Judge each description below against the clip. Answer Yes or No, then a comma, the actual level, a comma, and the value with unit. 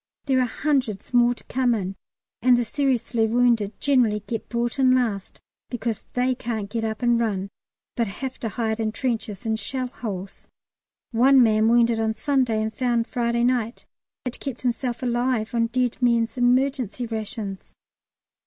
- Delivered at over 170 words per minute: No, average, 165 wpm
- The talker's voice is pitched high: Yes, high, 235 Hz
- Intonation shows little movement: Yes, narrow, 2.3 semitones